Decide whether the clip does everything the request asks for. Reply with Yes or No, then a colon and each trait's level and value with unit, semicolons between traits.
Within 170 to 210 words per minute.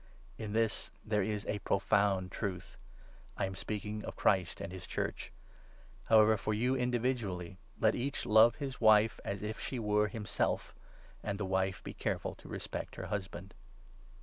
Yes: average, 175 wpm